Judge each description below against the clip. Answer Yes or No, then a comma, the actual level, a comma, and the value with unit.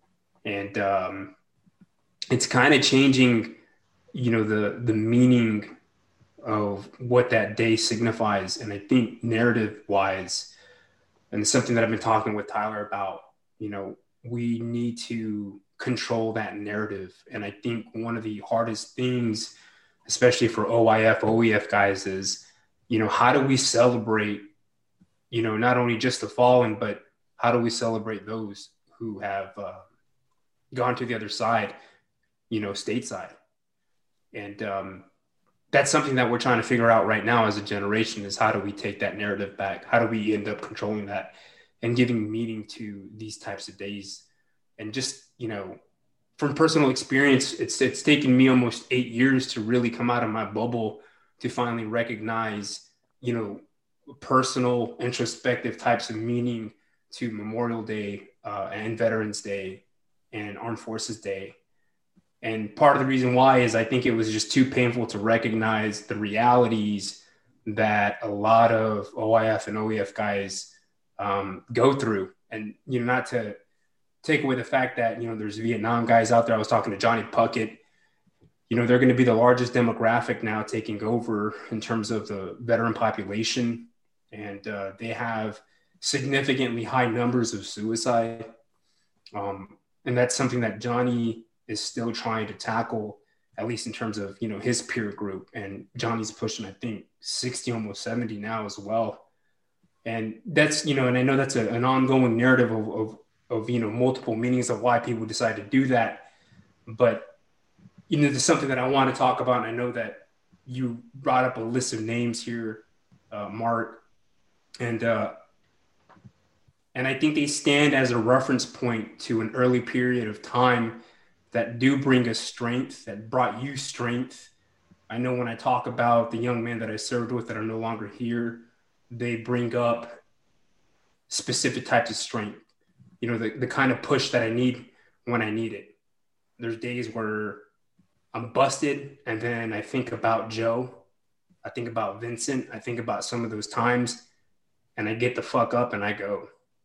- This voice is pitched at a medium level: No, low, 115 Hz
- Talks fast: No, average, 170 wpm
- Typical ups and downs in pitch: No, narrow, 2.3 semitones